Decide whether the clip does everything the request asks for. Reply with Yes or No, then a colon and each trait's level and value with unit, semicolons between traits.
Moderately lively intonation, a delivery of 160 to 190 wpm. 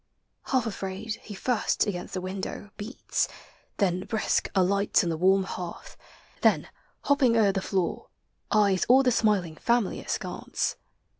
No: average, 3.1 semitones; average, 140 wpm